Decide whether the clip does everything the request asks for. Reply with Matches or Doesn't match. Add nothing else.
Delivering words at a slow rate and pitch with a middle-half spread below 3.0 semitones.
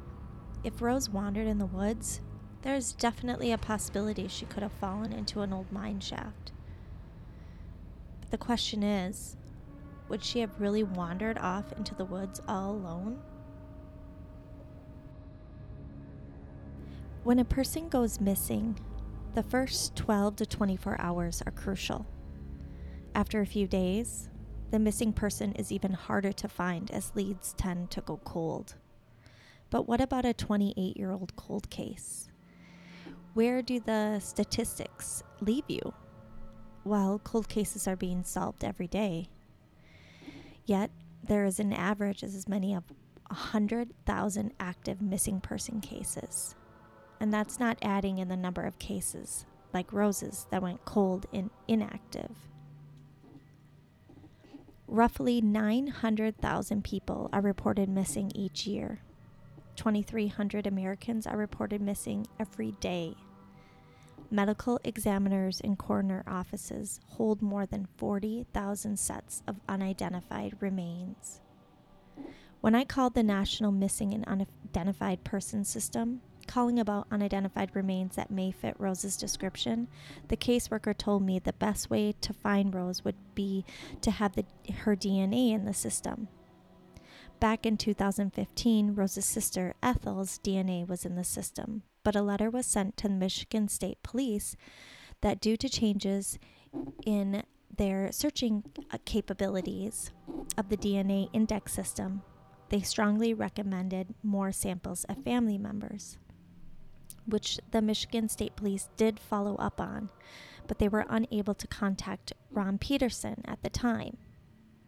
Matches